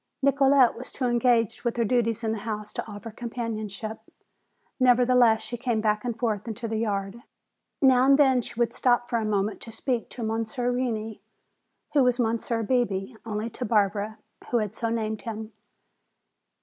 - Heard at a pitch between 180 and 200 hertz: No, high, 230 Hz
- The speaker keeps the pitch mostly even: Yes, narrow, 2.2 semitones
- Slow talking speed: No, average, 175 wpm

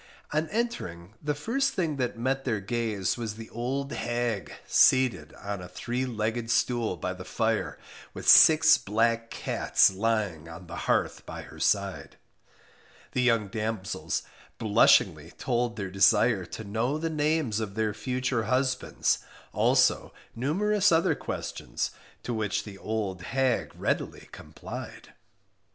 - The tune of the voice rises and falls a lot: No, average, 4.3 semitones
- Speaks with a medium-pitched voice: No, low, 115 Hz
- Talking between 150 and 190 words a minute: No, average, 140 wpm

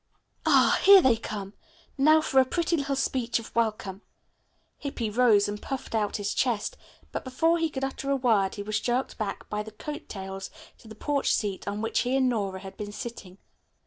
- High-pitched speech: Yes, high, 230 Hz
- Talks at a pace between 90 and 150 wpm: No, average, 200 wpm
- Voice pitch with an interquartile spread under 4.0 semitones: No, average, 4.6 semitones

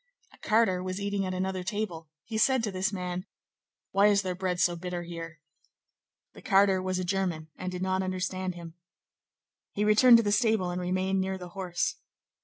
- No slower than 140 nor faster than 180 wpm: No, average, 190 wpm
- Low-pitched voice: No, medium, 185 Hz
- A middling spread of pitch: No, narrow, 1.8 semitones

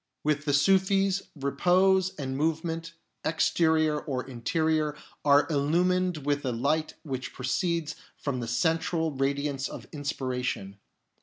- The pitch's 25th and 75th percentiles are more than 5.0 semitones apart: No, average, 3.1 semitones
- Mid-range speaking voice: Yes, medium, 150 Hz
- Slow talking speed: Yes, slow, 125 wpm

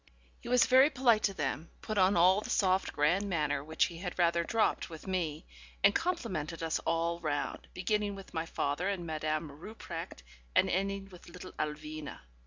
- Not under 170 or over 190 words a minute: Yes, average, 180 wpm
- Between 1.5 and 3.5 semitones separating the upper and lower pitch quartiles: No, average, 4.1 semitones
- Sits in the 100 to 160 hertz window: No, medium, 175 Hz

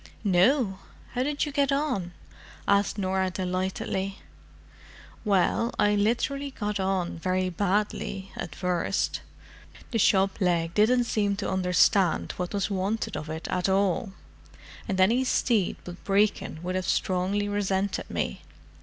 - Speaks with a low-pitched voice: No, high, 195 Hz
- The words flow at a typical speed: No, slow, 130 wpm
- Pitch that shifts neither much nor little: No, narrow, 2.3 semitones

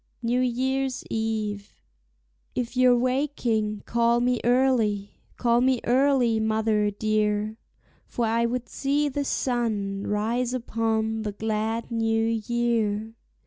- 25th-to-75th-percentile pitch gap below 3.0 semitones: Yes, narrow, 2.4 semitones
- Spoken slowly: Yes, slow, 115 wpm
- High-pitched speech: Yes, high, 230 Hz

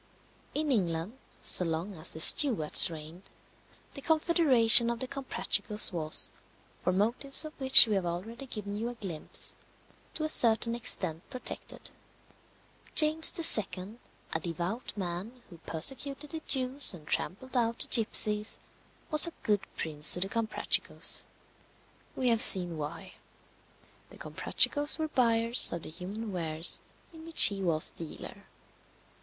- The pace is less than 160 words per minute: Yes, average, 140 wpm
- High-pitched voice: Yes, high, 220 Hz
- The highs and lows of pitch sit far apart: Yes, wide, 6.9 semitones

